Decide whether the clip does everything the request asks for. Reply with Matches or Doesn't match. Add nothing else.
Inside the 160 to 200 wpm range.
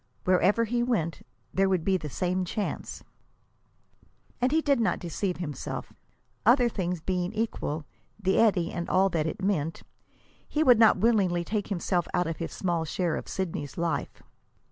Matches